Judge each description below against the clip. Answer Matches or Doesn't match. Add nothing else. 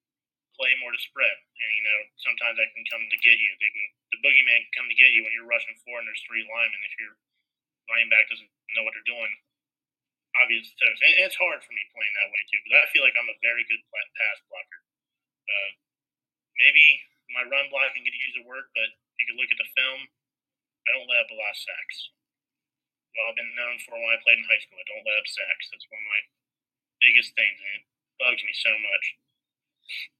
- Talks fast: Matches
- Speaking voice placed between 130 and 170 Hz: Matches